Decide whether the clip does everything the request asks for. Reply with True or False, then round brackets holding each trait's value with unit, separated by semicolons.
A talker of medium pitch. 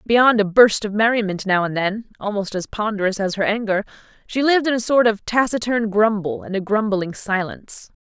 False (210 Hz)